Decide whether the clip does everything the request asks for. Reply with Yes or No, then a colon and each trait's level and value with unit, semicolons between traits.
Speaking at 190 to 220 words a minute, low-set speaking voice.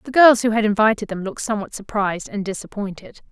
No: average, 200 wpm; high, 210 Hz